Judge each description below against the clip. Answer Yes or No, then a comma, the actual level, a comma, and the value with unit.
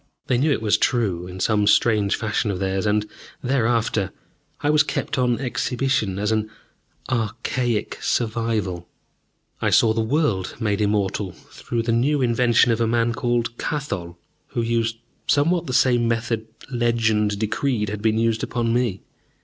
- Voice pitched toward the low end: Yes, low, 115 Hz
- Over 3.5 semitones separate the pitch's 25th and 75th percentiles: No, narrow, 2.5 semitones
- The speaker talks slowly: No, average, 155 wpm